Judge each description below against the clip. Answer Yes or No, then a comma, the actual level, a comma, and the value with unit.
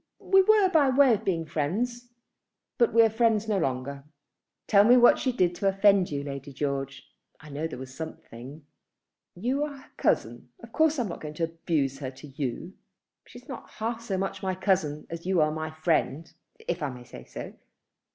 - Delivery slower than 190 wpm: No, average, 200 wpm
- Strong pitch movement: Yes, wide, 7.7 semitones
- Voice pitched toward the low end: No, medium, 175 Hz